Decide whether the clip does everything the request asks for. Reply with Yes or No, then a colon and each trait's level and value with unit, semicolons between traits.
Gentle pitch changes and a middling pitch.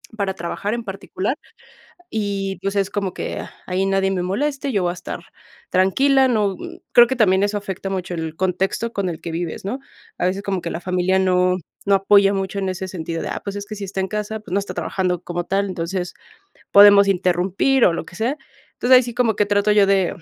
No: narrow, 2.1 semitones; high, 195 Hz